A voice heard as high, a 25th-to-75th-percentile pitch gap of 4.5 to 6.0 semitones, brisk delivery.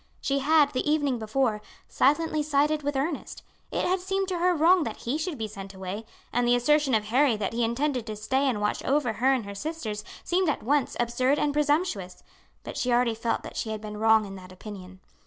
Yes: very high, 255 Hz; wide, 5.6 semitones; fast, 220 wpm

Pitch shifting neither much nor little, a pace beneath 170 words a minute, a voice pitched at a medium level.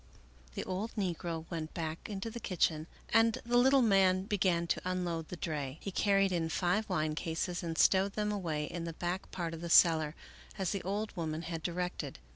No: average, 3.3 semitones; average, 195 wpm; medium, 180 Hz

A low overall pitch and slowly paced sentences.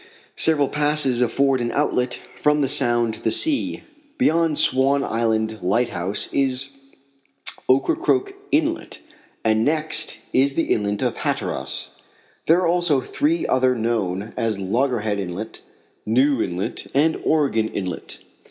Yes: low, 130 Hz; slow, 130 wpm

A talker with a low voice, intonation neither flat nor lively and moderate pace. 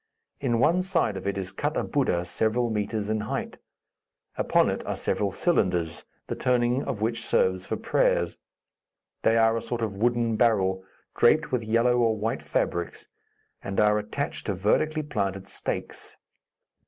Yes: low, 110 Hz; average, 3.7 semitones; average, 160 wpm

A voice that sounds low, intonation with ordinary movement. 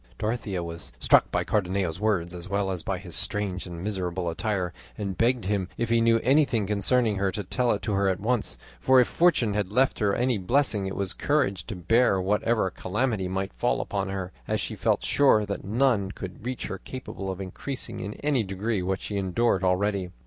Yes: low, 100 Hz; average, 3.7 semitones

